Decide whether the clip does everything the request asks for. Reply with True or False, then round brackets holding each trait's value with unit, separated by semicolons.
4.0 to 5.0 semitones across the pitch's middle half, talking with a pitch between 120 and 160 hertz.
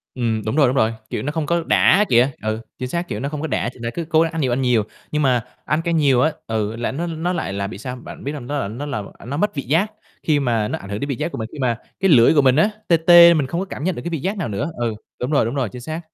False (5.5 semitones; 140 Hz)